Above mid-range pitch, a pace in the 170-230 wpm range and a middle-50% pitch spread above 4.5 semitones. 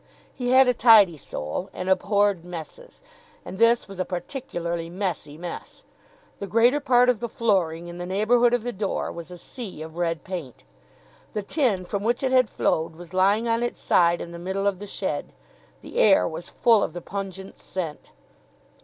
Yes: high, 195 Hz; average, 190 wpm; average, 5.2 semitones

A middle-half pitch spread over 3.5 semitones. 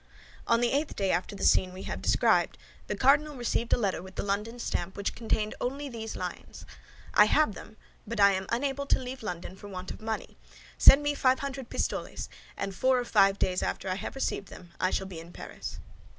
Yes: average, 5.2 semitones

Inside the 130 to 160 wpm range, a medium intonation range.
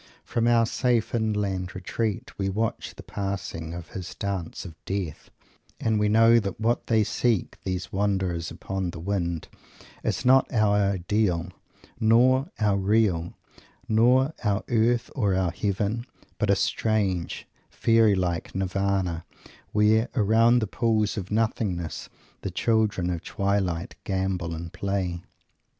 Yes: slow, 135 wpm; average, 3.3 semitones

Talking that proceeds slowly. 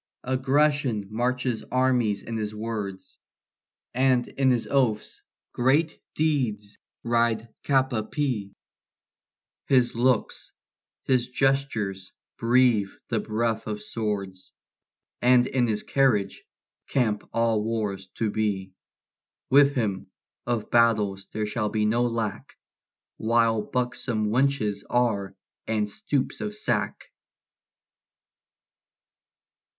Yes: slow, 105 wpm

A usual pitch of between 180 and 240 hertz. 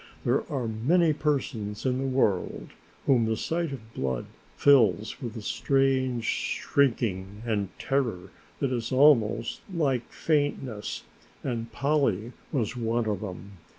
No: low, 120 Hz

